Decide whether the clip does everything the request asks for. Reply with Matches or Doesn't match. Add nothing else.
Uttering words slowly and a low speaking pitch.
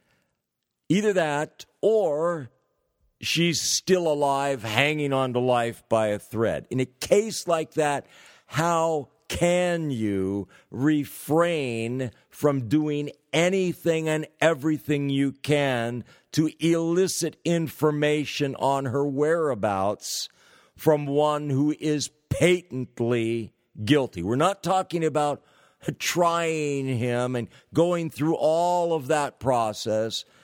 Doesn't match